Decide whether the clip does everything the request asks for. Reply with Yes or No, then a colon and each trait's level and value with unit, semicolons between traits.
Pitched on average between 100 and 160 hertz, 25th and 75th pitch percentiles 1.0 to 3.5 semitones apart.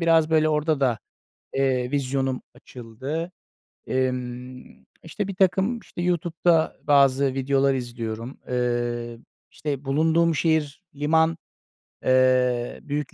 No: low, 135 Hz; average, 4.1 semitones